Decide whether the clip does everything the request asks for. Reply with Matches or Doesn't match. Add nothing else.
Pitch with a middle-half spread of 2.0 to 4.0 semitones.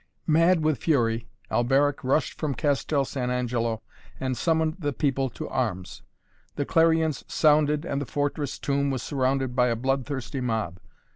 Matches